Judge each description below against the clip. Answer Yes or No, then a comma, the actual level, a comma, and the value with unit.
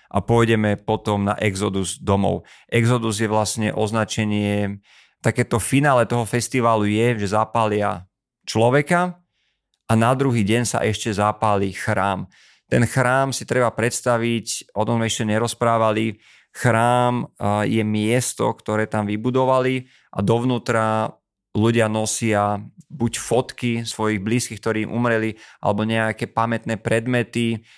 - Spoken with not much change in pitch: Yes, narrow, 2.0 semitones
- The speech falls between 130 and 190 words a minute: No, average, 120 wpm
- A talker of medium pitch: No, low, 115 Hz